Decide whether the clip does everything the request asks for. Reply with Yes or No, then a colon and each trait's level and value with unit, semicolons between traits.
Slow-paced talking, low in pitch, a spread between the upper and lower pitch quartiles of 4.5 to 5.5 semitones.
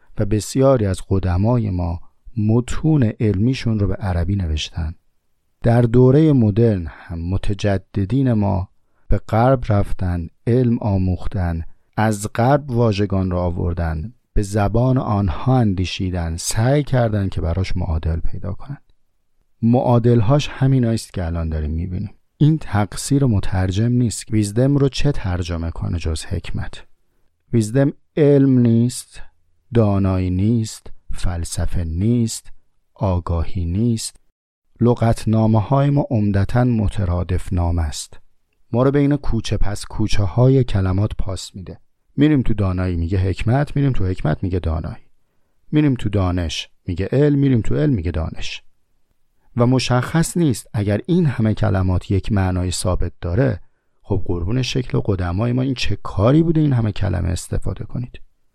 No: average, 130 wpm; low, 105 Hz; average, 5.1 semitones